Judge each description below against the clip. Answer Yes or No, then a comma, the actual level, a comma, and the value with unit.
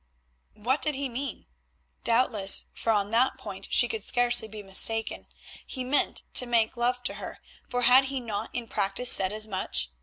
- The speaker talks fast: No, average, 180 wpm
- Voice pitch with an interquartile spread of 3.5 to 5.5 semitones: No, average, 3.0 semitones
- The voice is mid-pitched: No, high, 235 Hz